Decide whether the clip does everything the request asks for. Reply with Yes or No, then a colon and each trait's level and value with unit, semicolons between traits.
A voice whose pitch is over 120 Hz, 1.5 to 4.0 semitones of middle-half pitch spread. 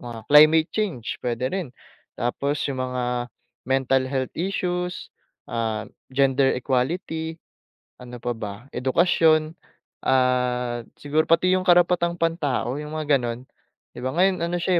No: medium, 140 Hz; average, 5.0 semitones